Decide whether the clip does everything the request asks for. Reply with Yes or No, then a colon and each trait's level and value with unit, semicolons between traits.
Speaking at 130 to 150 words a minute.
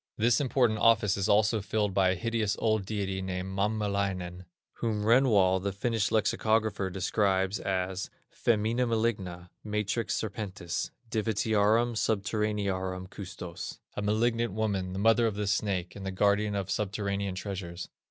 Yes: slow, 135 wpm